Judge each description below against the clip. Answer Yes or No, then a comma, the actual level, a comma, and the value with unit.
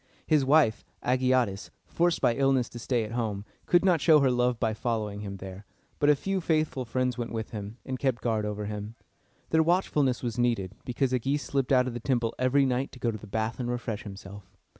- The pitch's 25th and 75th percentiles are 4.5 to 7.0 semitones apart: No, average, 3.7 semitones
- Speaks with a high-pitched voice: No, low, 120 Hz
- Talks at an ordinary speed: No, fast, 225 wpm